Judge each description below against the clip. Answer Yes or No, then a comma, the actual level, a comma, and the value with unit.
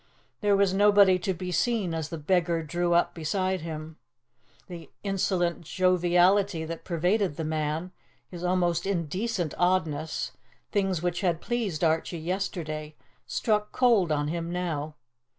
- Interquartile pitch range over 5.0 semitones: No, average, 2.9 semitones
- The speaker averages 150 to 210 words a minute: No, slow, 135 wpm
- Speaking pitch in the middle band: Yes, medium, 175 Hz